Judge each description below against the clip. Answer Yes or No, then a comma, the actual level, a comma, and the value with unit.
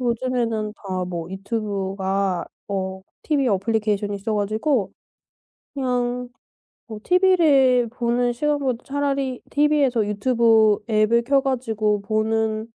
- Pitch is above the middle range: Yes, high, 225 Hz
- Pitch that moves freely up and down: No, average, 3.8 semitones